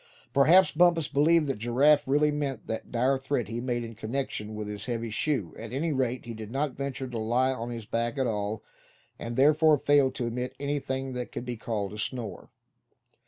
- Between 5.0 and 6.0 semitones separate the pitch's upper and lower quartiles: No, average, 3.6 semitones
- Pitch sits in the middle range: No, low, 125 Hz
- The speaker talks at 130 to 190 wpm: No, average, 200 wpm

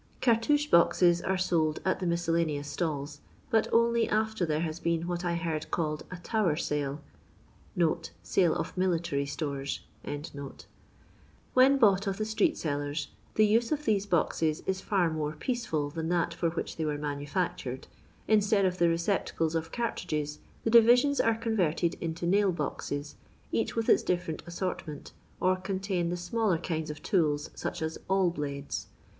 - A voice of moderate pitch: Yes, medium, 170 Hz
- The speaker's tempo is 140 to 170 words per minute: Yes, average, 160 wpm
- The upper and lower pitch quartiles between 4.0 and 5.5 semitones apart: Yes, average, 4.3 semitones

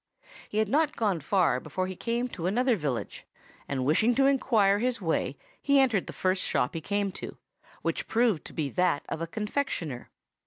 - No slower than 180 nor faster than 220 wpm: Yes, average, 190 wpm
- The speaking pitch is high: Yes, high, 200 Hz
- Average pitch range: No, wide, 6.4 semitones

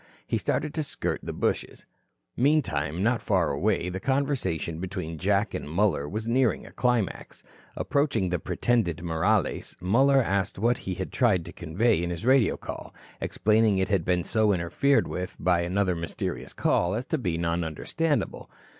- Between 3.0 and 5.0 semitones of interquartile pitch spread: No, wide, 5.6 semitones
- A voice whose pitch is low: Yes, very low, 95 Hz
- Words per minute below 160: No, average, 165 wpm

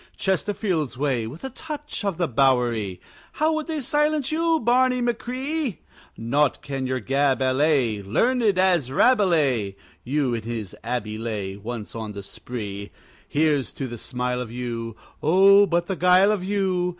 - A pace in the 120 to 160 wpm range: Yes, average, 155 wpm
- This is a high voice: No, medium, 145 Hz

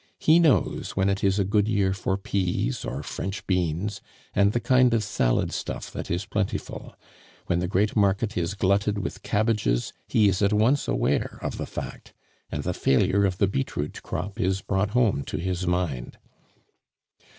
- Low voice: Yes, low, 100 Hz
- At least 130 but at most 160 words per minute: No, average, 175 wpm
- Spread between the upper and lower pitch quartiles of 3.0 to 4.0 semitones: No, narrow, 2.5 semitones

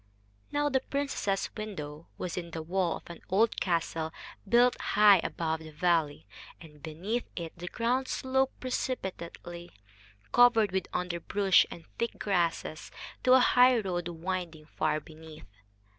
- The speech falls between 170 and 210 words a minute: No, slow, 135 wpm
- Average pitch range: No, wide, 5.9 semitones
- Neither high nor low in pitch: Yes, medium, 180 Hz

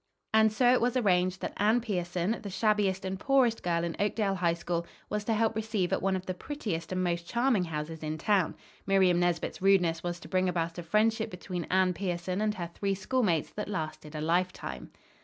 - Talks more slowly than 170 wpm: No, fast, 205 wpm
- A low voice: No, medium, 185 Hz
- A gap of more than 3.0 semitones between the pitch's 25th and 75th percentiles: Yes, average, 3.7 semitones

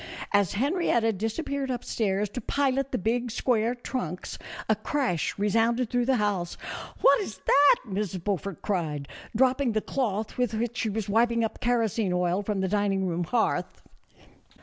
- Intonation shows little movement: No, average, 3.8 semitones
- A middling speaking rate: Yes, average, 160 wpm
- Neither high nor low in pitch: No, high, 220 Hz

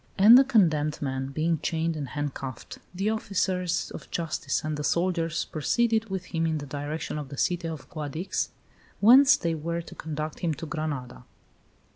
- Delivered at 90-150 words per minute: No, average, 170 wpm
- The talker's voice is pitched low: No, medium, 160 Hz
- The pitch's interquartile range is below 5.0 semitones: Yes, average, 3.5 semitones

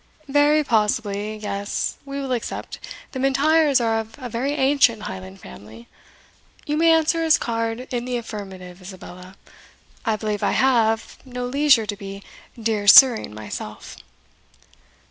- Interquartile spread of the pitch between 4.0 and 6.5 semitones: Yes, average, 4.9 semitones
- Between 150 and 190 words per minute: No, average, 140 wpm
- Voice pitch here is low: No, high, 230 Hz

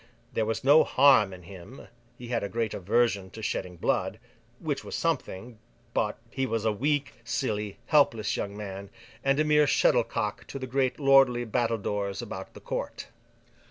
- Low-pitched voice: Yes, low, 115 Hz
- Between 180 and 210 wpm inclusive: No, average, 160 wpm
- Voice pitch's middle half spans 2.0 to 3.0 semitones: No, average, 4.4 semitones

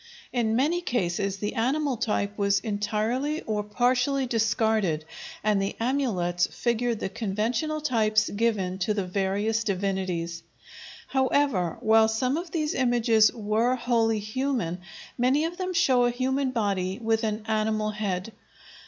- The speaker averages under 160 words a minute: Yes, slow, 135 wpm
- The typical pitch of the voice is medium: No, high, 220 Hz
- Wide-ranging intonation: No, average, 3.8 semitones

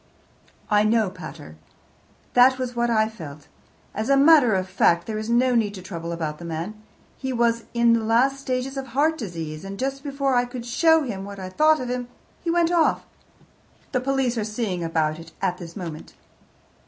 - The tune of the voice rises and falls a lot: Yes, wide, 6.1 semitones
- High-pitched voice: Yes, high, 230 Hz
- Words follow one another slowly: No, average, 195 wpm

